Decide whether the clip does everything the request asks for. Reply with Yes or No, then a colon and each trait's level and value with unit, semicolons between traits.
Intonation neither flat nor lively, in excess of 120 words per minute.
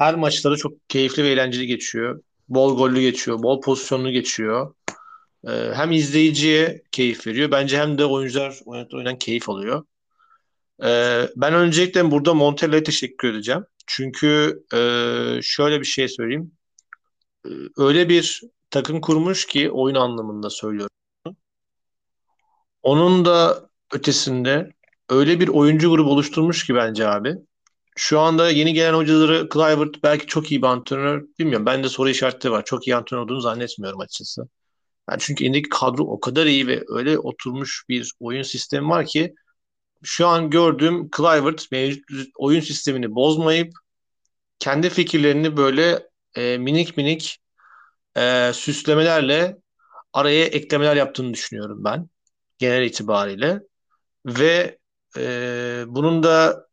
Yes: average, 4.0 semitones; average, 130 wpm